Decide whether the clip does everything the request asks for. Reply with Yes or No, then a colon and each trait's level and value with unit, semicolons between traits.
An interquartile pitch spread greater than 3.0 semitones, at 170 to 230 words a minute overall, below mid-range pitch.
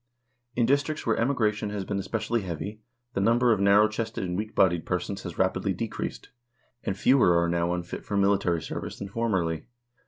Yes: average, 4.0 semitones; average, 180 wpm; low, 100 Hz